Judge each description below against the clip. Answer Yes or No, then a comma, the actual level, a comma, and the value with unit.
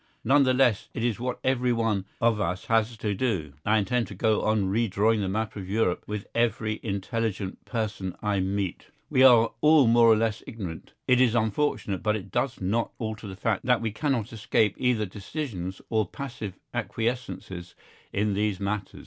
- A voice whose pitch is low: Yes, low, 110 Hz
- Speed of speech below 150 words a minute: No, average, 180 wpm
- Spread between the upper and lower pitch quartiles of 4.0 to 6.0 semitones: No, average, 3.0 semitones